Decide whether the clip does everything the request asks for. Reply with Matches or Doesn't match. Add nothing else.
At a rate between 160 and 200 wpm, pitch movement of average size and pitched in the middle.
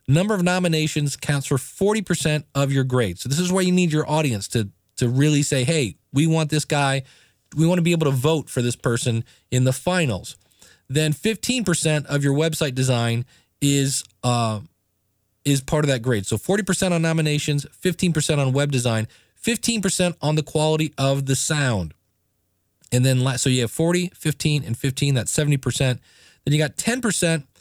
Matches